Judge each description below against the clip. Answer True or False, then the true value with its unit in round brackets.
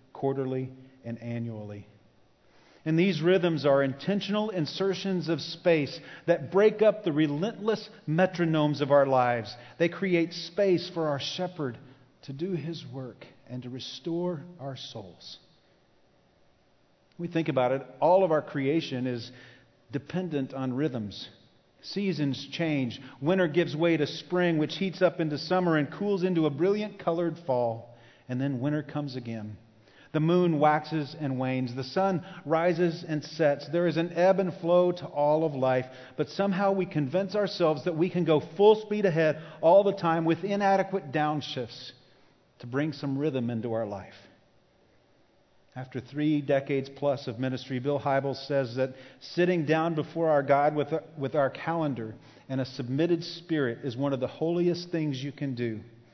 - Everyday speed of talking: True (155 wpm)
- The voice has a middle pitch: True (150 Hz)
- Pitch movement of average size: True (4.7 semitones)